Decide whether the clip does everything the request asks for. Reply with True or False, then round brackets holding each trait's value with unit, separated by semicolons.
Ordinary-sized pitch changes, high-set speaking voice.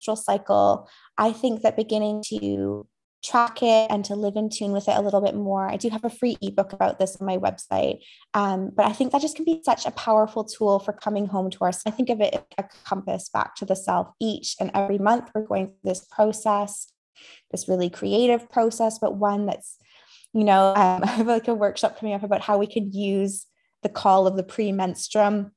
False (2.1 semitones; 205 Hz)